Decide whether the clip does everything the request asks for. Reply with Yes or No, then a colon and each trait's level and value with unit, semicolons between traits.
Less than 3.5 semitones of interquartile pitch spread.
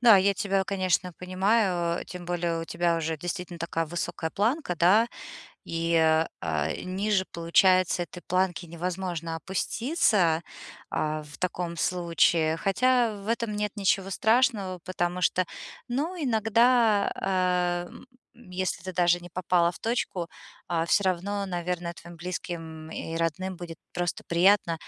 Yes: average, 2.7 semitones